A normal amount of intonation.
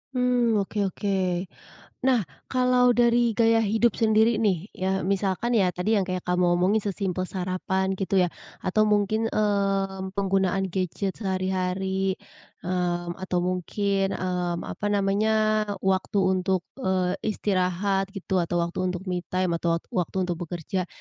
No: narrow, 2.2 semitones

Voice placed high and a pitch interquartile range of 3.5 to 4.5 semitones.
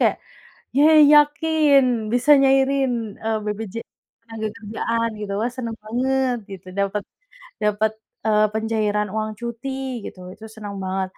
Yes: high, 225 Hz; average, 4.0 semitones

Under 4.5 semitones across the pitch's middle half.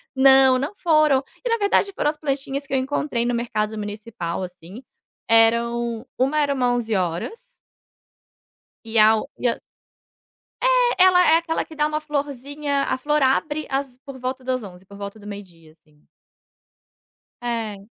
No: average, 5.2 semitones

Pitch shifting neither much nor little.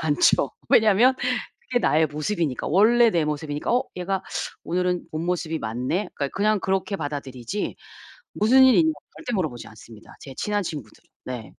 No: wide, 6.4 semitones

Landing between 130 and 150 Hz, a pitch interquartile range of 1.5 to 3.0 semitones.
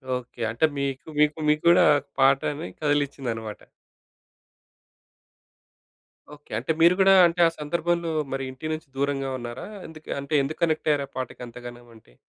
No: medium, 140 Hz; average, 3.8 semitones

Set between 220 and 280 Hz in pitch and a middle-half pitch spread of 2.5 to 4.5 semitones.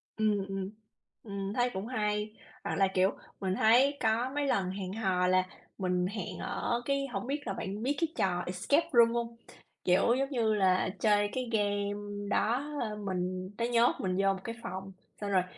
No: high, 205 Hz; average, 3.6 semitones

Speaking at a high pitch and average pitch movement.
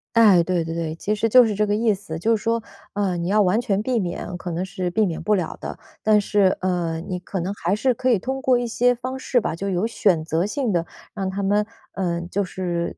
Yes: high, 200 Hz; average, 3.9 semitones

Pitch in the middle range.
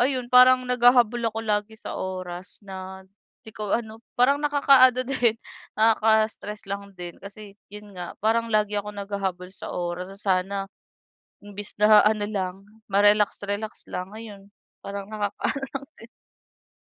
No: high, 210 Hz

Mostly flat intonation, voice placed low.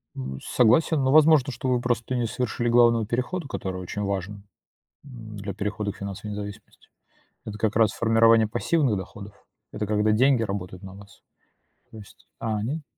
No: average, 3.3 semitones; low, 110 Hz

